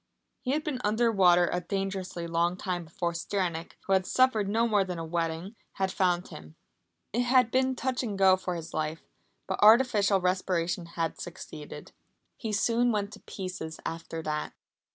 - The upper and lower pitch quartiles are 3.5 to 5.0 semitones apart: Yes, average, 4.2 semitones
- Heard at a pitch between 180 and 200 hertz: Yes, high, 190 Hz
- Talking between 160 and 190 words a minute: Yes, average, 175 wpm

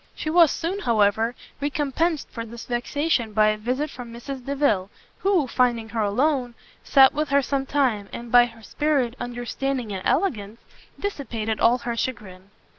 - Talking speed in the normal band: Yes, average, 160 wpm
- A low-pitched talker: No, high, 245 Hz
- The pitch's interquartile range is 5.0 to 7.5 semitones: No, average, 3.9 semitones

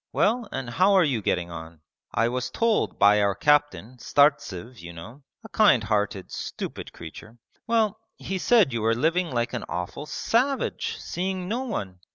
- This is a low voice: Yes, low, 130 Hz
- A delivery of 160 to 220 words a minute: Yes, average, 170 wpm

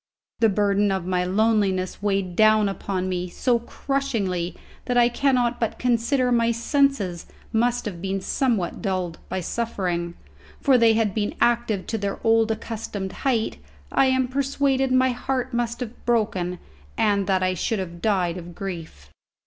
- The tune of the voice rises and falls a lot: No, average, 4.5 semitones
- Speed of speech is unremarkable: Yes, average, 155 wpm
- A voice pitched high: Yes, high, 215 Hz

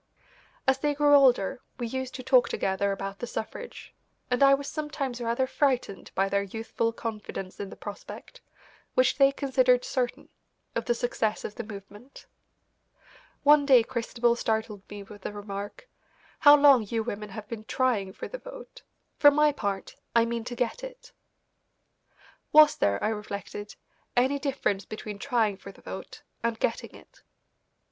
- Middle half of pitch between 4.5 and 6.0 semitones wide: Yes, average, 4.8 semitones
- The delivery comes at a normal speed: Yes, average, 160 wpm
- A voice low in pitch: No, high, 235 Hz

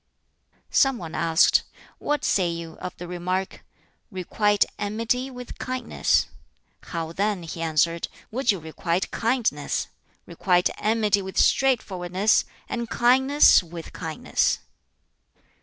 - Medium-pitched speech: No, high, 195 Hz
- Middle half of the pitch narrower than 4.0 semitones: No, wide, 5.5 semitones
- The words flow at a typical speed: No, slow, 110 wpm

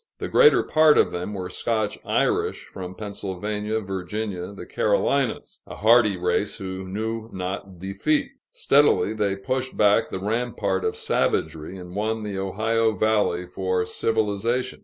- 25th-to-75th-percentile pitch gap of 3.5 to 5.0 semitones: No, average, 2.9 semitones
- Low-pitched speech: Yes, low, 105 Hz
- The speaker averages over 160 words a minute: No, average, 140 wpm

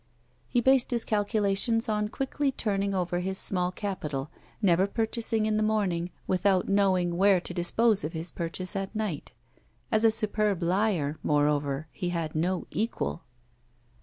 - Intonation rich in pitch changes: No, average, 3.7 semitones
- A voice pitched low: No, high, 195 Hz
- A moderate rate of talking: Yes, average, 150 wpm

